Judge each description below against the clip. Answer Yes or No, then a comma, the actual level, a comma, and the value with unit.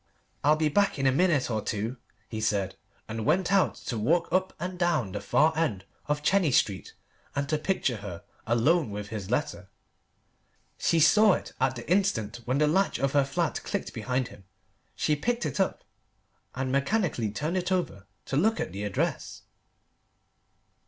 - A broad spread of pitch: Yes, wide, 8.0 semitones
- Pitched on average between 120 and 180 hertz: Yes, medium, 140 Hz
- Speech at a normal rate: Yes, average, 175 wpm